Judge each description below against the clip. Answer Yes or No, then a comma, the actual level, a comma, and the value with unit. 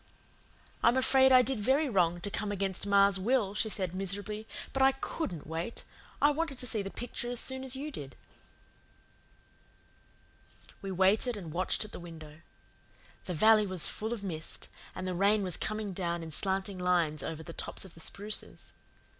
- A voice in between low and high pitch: No, high, 200 Hz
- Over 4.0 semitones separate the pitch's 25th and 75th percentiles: Yes, average, 4.7 semitones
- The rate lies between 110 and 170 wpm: No, average, 180 wpm